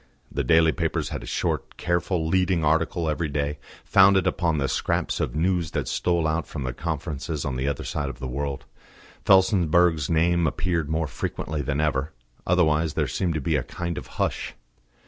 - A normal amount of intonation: Yes, average, 3.2 semitones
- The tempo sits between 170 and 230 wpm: Yes, average, 185 wpm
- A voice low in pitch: Yes, very low, 80 Hz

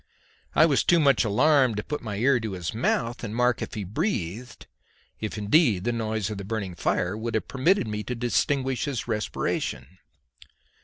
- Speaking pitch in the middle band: No, low, 115 Hz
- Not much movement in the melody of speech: No, average, 3.9 semitones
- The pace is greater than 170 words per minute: Yes, average, 185 wpm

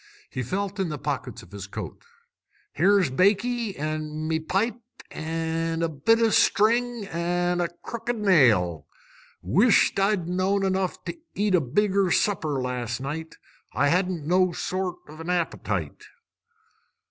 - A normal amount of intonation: Yes, average, 4.2 semitones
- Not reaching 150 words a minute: Yes, average, 140 wpm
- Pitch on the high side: No, medium, 180 Hz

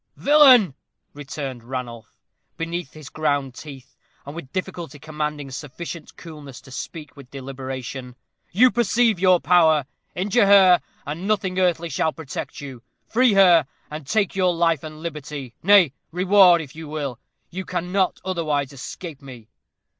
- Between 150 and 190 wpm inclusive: No, average, 140 wpm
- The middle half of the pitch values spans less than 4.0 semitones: No, average, 4.8 semitones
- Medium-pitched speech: Yes, medium, 155 Hz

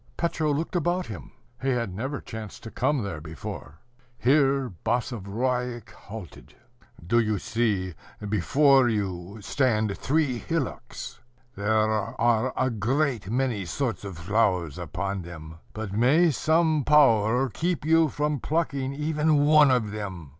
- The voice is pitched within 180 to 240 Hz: No, low, 120 Hz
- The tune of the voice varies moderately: No, wide, 5.8 semitones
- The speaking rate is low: Yes, slow, 130 wpm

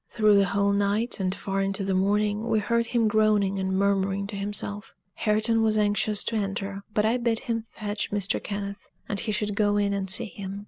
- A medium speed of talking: No, fast, 210 wpm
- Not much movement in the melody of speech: Yes, narrow, 1.4 semitones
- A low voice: No, high, 205 Hz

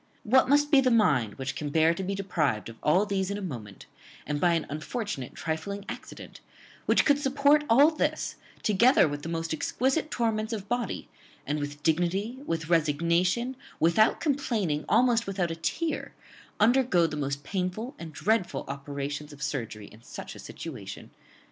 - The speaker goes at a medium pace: Yes, average, 165 wpm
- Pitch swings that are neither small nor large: No, wide, 7.6 semitones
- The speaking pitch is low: No, medium, 180 Hz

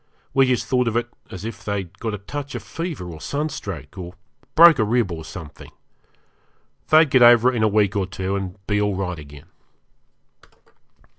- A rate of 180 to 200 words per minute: Yes, average, 190 wpm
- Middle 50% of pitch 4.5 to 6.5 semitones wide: Yes, average, 5.2 semitones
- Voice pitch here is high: No, low, 105 Hz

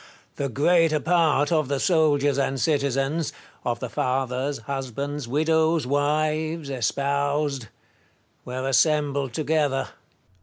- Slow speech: Yes, slow, 115 wpm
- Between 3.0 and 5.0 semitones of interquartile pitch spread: No, narrow, 2.4 semitones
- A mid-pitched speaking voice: Yes, medium, 145 Hz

